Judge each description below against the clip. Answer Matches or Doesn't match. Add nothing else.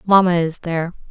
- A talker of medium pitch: Matches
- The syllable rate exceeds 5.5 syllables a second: Matches